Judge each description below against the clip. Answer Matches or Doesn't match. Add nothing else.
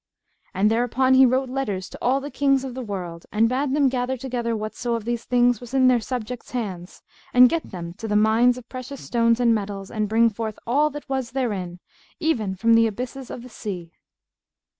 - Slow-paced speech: Doesn't match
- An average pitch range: Matches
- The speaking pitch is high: Matches